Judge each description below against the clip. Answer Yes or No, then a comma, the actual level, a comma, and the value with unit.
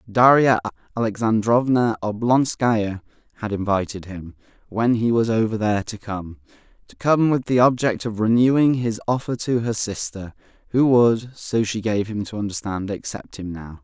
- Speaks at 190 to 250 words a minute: No, average, 155 wpm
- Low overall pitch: Yes, low, 110 Hz